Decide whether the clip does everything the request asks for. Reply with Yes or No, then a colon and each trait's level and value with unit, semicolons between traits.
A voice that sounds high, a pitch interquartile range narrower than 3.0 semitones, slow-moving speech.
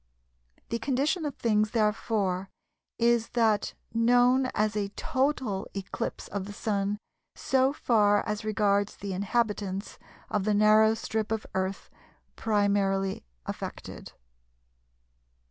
Yes: high, 215 Hz; narrow, 2.5 semitones; slow, 110 wpm